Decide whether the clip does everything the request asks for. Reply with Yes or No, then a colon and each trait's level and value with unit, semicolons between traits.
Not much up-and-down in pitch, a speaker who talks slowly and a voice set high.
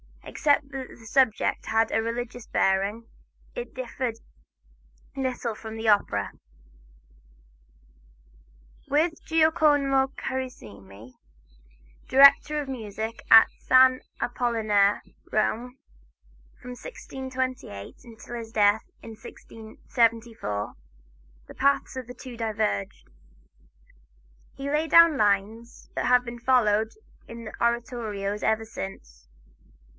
No: average, 3.3 semitones; slow, 100 wpm; high, 235 Hz